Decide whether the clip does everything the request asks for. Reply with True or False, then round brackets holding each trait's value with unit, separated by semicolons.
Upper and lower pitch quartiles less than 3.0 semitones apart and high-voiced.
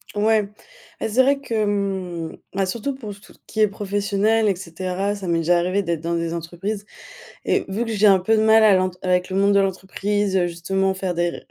True (2.5 semitones; 195 Hz)